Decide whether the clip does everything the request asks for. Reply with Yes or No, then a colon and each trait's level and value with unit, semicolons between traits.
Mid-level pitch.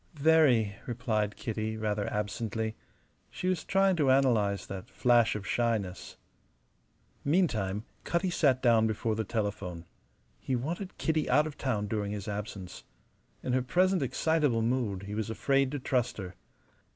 No: low, 115 Hz